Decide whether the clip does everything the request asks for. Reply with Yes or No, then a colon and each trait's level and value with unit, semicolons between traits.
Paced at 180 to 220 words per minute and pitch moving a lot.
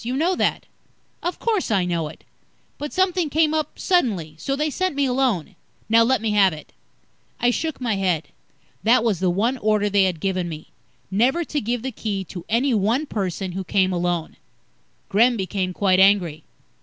Yes: average, 185 wpm; wide, 6.3 semitones